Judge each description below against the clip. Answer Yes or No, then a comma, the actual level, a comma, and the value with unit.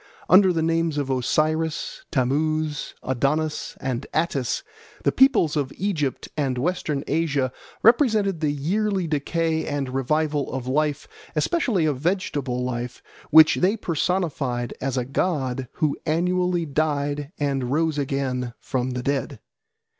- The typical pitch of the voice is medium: Yes, medium, 150 Hz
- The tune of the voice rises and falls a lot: No, average, 3.7 semitones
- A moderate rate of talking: No, slow, 130 wpm